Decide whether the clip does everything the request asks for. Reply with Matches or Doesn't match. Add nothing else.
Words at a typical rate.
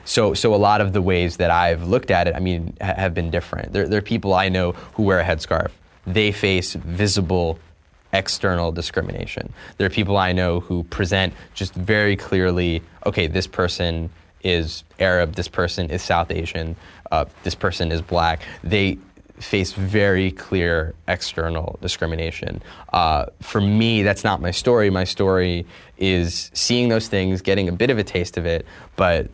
Matches